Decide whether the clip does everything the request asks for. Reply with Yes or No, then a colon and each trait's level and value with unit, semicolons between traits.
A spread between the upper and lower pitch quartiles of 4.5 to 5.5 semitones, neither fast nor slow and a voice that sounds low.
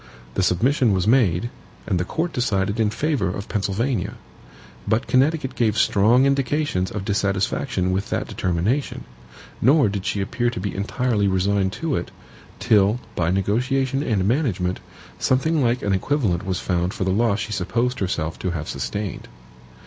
Yes: average, 5.1 semitones; average, 155 wpm; low, 105 Hz